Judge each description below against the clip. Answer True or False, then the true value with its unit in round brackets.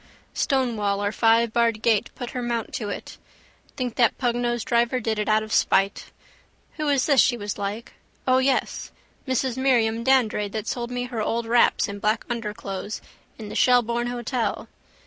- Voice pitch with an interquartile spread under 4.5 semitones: True (2.4 semitones)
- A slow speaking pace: False (165 wpm)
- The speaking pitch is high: True (235 Hz)